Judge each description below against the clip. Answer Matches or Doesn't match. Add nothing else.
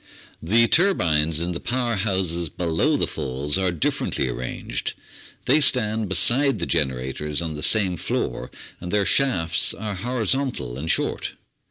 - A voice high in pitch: Doesn't match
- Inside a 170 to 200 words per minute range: Doesn't match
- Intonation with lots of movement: Matches